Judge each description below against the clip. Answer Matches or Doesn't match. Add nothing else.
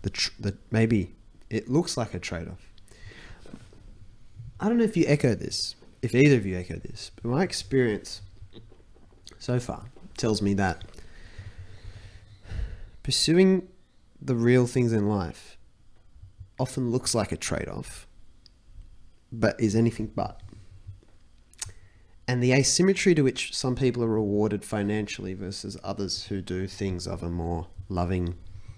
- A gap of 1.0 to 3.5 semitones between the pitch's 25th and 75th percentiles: Doesn't match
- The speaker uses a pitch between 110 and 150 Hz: Doesn't match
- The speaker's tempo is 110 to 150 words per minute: Matches